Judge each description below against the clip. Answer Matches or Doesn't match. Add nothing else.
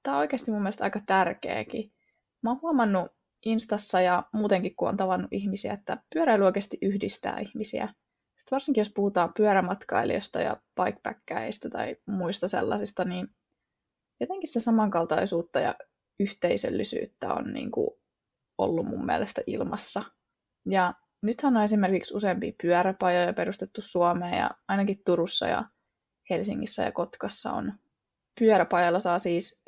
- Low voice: Doesn't match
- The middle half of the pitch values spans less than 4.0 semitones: Matches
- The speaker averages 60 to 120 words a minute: Doesn't match